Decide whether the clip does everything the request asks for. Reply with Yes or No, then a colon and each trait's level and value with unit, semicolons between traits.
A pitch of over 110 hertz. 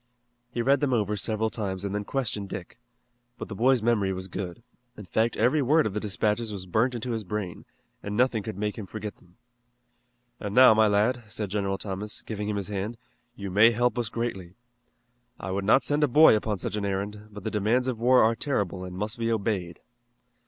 No: low, 105 Hz